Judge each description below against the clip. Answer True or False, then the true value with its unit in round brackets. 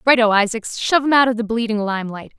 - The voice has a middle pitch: False (225 Hz)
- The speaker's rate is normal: False (225 wpm)